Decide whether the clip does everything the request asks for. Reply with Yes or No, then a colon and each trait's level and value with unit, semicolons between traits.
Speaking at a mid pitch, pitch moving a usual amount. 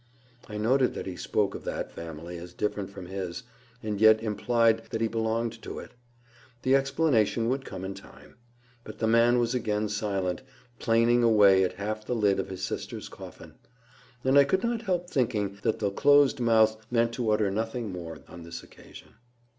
No: low, 110 Hz; average, 3.3 semitones